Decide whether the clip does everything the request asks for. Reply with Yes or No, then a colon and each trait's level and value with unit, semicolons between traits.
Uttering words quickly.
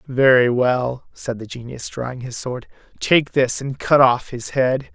No: average, 180 wpm